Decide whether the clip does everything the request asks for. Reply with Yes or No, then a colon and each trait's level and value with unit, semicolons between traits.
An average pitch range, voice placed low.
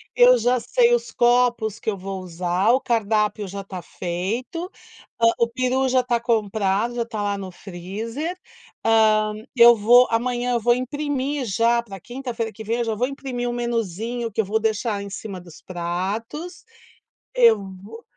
No: average, 3.6 semitones; high, 230 Hz